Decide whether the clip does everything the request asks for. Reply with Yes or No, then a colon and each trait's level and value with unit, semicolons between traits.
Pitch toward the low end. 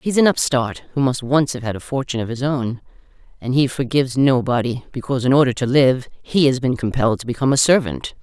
Yes: low, 130 Hz